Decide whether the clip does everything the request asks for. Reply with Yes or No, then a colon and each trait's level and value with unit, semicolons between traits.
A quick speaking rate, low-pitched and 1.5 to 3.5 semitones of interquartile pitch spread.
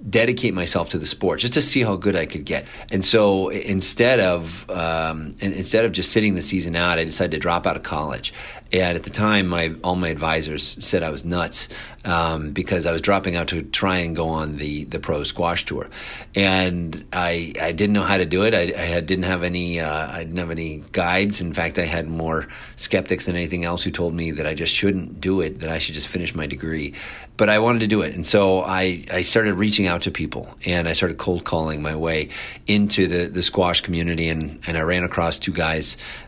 Yes: fast, 235 wpm; very low, 90 Hz; average, 2.7 semitones